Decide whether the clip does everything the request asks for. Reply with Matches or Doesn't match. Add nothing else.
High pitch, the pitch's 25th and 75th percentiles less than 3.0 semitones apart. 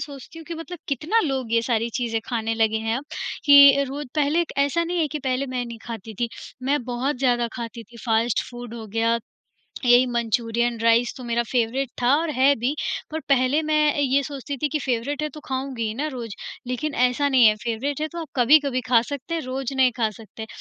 Doesn't match